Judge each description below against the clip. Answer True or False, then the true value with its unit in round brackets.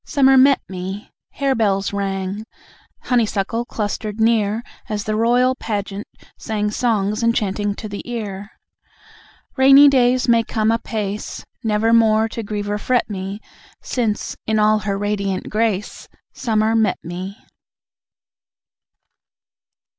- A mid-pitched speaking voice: False (215 Hz)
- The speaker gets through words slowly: True (115 wpm)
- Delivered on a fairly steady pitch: True (2.2 semitones)